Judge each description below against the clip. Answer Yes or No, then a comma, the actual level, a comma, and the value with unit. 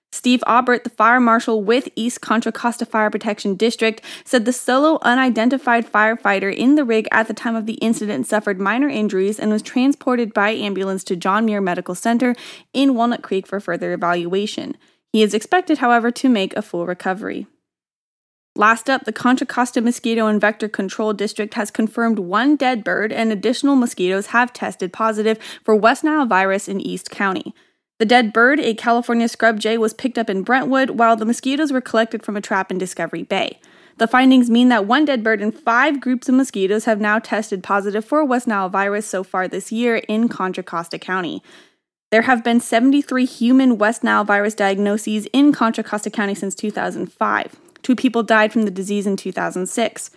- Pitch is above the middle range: Yes, high, 225 Hz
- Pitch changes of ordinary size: Yes, average, 3.2 semitones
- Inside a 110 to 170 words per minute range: No, average, 185 wpm